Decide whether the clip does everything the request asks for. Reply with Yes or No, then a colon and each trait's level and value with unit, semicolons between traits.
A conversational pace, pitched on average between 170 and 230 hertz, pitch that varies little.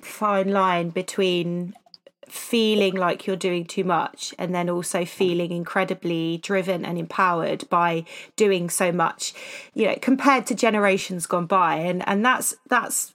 Yes: average, 145 wpm; medium, 185 Hz; narrow, 2.3 semitones